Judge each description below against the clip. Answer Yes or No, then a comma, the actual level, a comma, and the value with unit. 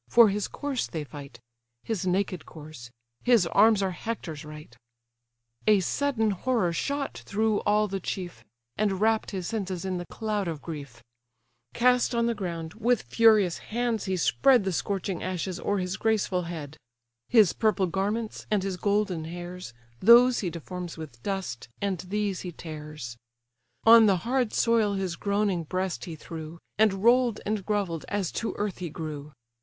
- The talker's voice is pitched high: Yes, high, 195 Hz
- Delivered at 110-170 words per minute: Yes, average, 160 wpm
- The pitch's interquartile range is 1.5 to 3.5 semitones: No, average, 4.4 semitones